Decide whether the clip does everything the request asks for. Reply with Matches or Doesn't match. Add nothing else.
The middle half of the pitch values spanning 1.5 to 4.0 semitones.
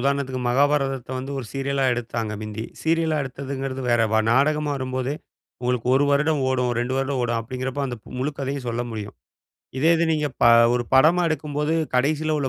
Matches